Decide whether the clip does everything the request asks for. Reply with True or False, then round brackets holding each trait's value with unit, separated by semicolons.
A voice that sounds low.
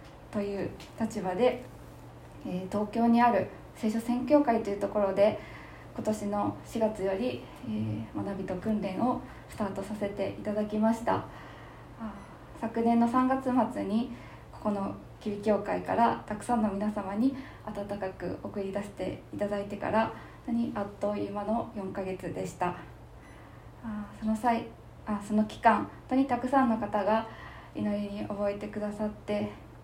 False (210 Hz)